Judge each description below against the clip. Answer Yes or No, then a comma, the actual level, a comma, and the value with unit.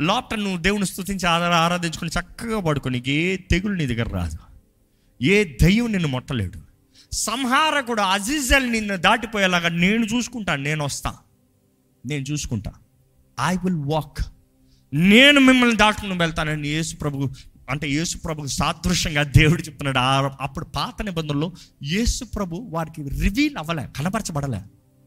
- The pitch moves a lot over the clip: Yes, wide, 6.3 semitones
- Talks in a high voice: No, medium, 165 Hz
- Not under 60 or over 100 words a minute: No, average, 120 wpm